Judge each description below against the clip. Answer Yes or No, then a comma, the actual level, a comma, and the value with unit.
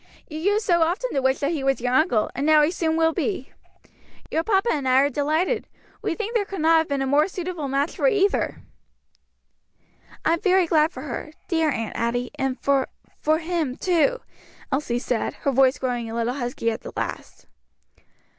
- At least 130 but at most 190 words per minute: No, average, 200 wpm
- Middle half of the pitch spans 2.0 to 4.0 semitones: No, average, 4.7 semitones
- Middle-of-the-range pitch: No, very high, 305 Hz